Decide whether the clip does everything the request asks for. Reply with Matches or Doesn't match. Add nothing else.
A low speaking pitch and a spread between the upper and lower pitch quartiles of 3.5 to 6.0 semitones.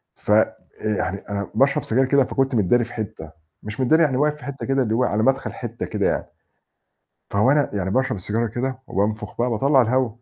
Matches